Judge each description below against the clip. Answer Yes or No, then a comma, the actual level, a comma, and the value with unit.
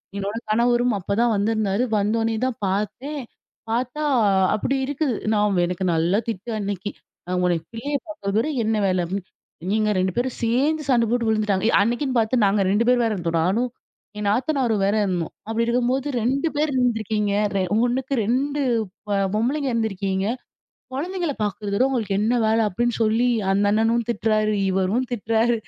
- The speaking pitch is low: No, high, 225 Hz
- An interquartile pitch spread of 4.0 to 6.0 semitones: No, average, 3.6 semitones